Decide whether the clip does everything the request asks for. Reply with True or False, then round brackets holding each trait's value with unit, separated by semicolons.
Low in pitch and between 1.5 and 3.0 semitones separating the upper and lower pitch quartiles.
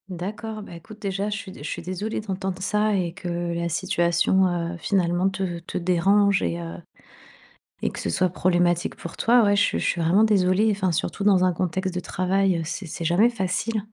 False (185 Hz; 2.7 semitones)